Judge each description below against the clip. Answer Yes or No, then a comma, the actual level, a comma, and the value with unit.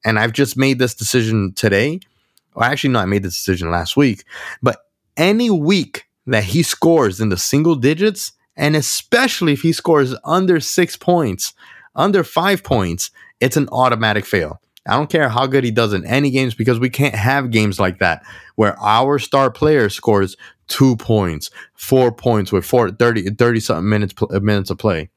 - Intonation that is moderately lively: No, wide, 6.0 semitones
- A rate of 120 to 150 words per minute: No, average, 180 wpm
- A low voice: Yes, low, 125 Hz